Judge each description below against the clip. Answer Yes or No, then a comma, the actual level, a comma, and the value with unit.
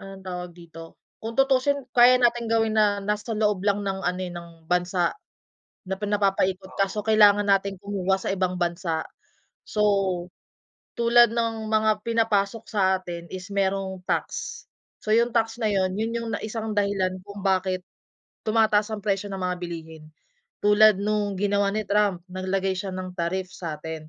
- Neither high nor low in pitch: No, high, 200 Hz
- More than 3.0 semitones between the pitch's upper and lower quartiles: No, average, 2.7 semitones